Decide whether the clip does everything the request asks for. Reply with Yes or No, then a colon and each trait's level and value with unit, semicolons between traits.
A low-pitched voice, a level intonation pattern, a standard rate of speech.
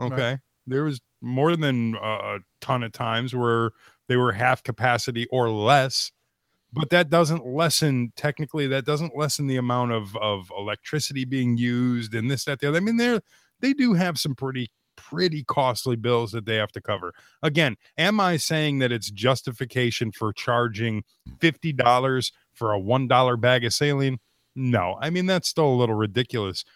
No: low, 125 Hz; average, 3.8 semitones; average, 170 wpm